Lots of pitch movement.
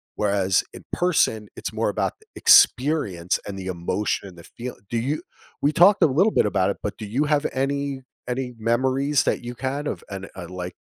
Yes: wide, 6.4 semitones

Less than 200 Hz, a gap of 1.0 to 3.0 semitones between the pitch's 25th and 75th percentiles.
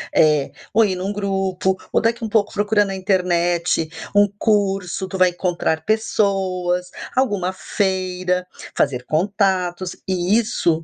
Yes: high, 190 Hz; narrow, 2.4 semitones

